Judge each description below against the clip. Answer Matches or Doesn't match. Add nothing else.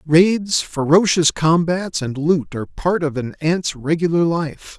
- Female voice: Doesn't match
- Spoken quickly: Doesn't match